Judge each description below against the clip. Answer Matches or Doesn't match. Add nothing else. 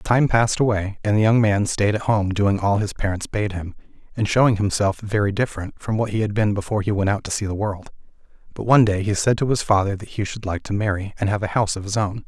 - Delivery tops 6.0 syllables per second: Matches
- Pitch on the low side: Matches